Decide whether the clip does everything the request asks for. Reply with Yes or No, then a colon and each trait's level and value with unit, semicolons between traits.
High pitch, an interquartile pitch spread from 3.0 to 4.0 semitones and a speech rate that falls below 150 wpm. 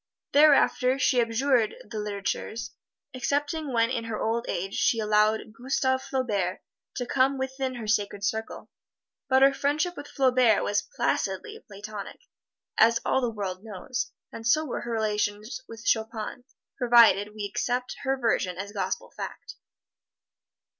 Yes: high, 230 Hz; average, 3.7 semitones; average, 140 wpm